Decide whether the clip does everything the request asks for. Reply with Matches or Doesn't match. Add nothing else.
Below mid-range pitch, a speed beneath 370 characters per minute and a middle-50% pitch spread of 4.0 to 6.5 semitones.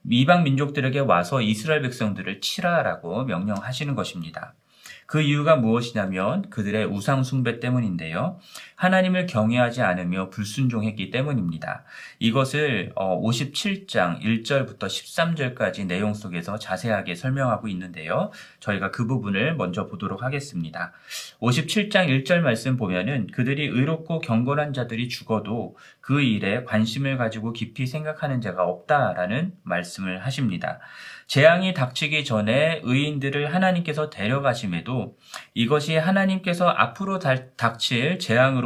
Matches